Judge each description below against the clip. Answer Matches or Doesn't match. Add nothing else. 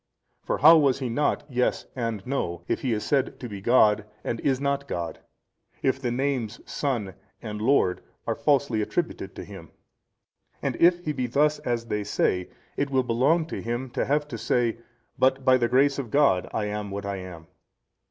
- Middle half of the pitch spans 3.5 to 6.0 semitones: Matches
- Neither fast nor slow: Matches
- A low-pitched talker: Matches